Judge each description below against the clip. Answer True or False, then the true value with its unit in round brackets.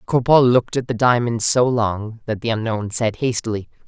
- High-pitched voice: False (115 Hz)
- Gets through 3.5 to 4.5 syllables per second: False (5.4 syllables/s)